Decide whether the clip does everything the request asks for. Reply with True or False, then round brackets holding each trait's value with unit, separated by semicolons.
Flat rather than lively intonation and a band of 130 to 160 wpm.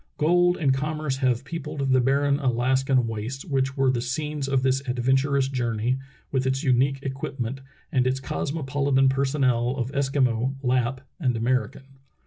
True (1.7 semitones; 150 wpm)